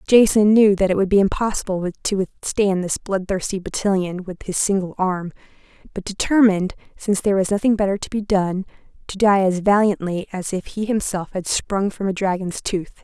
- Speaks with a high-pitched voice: Yes, high, 195 Hz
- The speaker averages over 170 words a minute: Yes, average, 190 wpm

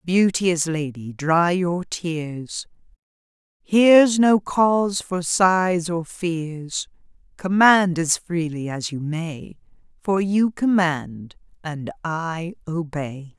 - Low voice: No, medium, 170 Hz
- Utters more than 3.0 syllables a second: No, 2.9 syllables/s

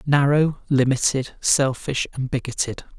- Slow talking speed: Yes, slow, 100 wpm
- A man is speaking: Yes, male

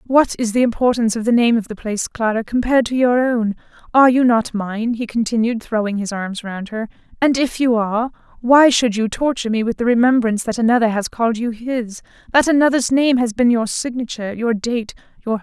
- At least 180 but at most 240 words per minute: Yes, fast, 205 wpm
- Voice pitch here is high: Yes, high, 235 Hz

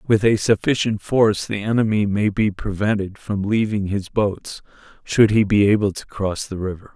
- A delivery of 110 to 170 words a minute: No, average, 180 wpm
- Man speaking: Yes, male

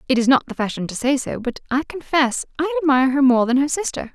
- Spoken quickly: Yes, fast, 260 wpm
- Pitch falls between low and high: No, very high, 275 Hz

